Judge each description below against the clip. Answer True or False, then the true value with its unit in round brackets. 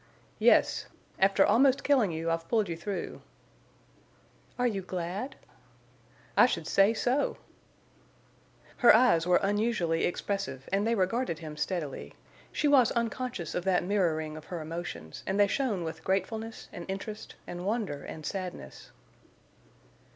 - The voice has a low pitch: False (190 Hz)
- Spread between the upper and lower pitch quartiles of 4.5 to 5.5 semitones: True (5.2 semitones)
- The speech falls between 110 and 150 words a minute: True (135 wpm)